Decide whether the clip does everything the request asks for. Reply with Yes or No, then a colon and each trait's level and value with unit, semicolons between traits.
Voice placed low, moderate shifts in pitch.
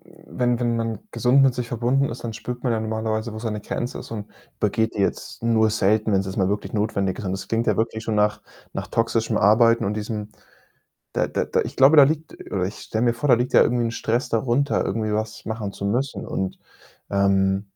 No: low, 110 Hz; narrow, 2.3 semitones